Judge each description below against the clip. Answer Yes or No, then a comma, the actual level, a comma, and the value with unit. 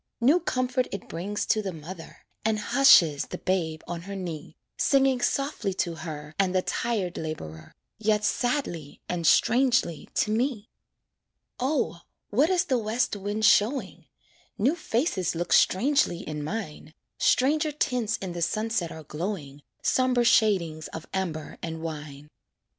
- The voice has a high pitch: Yes, high, 200 Hz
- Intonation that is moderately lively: No, wide, 7.0 semitones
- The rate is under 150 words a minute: Yes, average, 140 wpm